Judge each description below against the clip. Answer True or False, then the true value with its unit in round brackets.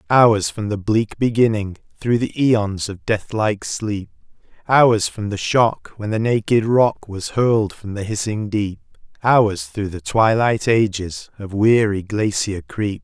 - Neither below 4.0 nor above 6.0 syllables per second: False (3.8 syllables/s)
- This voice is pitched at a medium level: False (105 Hz)